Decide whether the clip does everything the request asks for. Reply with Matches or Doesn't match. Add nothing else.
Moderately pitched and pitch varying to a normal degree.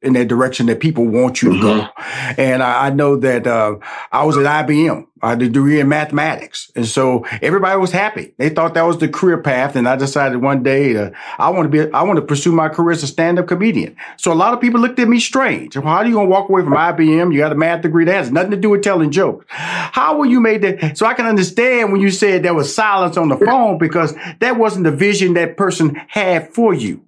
Doesn't match